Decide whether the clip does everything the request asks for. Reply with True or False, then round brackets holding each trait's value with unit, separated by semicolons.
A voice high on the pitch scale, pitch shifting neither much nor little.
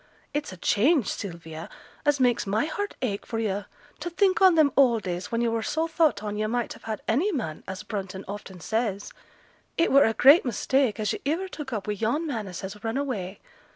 False (225 Hz; 6.0 semitones)